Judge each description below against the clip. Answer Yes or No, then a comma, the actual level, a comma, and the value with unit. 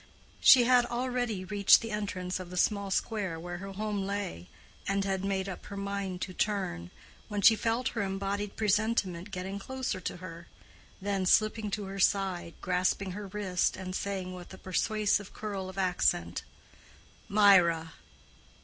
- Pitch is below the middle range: No, high, 195 Hz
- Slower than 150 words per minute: No, average, 160 wpm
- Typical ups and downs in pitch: No, narrow, 2.2 semitones